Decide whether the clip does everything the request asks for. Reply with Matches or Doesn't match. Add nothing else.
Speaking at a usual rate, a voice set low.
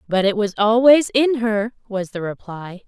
Doesn't match